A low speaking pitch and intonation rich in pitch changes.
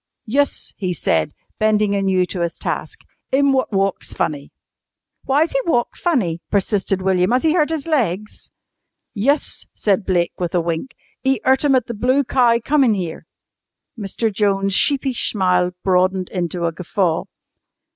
No: high, 205 Hz; wide, 6.3 semitones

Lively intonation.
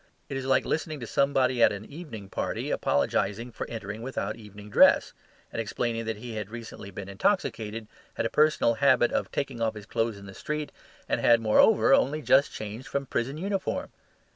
No: average, 4.6 semitones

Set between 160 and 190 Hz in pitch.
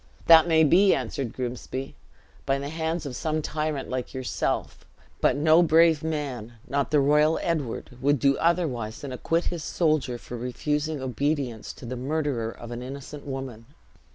No: medium, 140 Hz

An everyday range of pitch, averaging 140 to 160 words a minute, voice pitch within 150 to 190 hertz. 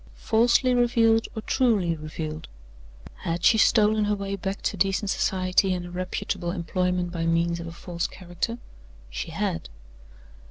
Yes: average, 3.8 semitones; average, 150 wpm; medium, 185 Hz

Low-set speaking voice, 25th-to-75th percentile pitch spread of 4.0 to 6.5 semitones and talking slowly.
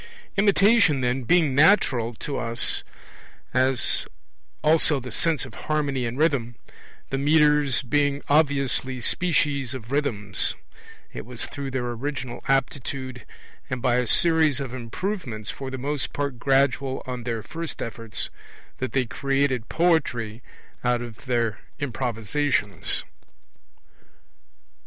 No: low, 130 Hz; average, 3.2 semitones; slow, 120 wpm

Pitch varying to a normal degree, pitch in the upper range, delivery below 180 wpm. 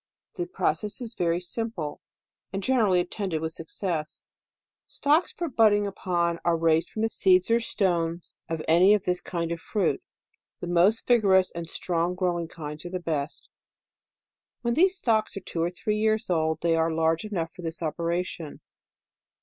No: average, 4.2 semitones; medium, 180 Hz; average, 170 wpm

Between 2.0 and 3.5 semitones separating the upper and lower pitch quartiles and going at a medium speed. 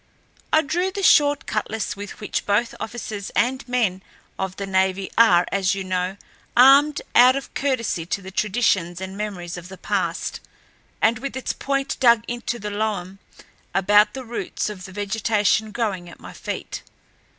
No: average, 4.2 semitones; average, 165 wpm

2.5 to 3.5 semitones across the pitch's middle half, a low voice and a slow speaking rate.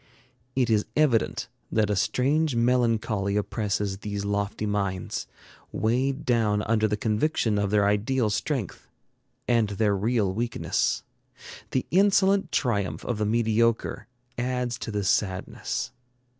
Yes: average, 3.1 semitones; low, 110 Hz; slow, 125 wpm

